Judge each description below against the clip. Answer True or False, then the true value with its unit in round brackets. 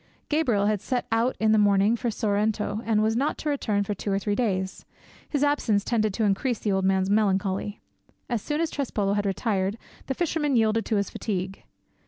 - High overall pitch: True (215 Hz)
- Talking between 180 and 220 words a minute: True (200 wpm)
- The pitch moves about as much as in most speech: True (3.0 semitones)